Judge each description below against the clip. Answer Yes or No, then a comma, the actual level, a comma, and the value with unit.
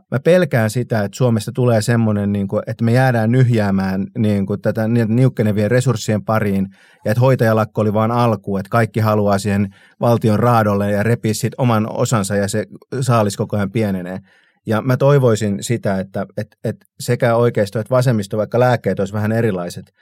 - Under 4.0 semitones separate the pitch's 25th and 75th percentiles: Yes, narrow, 2.5 semitones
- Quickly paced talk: Yes, fast, 160 wpm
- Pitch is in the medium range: No, low, 110 Hz